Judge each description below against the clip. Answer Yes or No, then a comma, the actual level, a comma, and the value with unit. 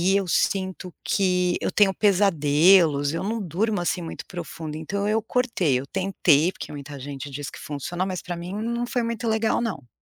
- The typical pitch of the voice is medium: Yes, medium, 180 Hz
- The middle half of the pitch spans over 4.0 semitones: Yes, average, 4.8 semitones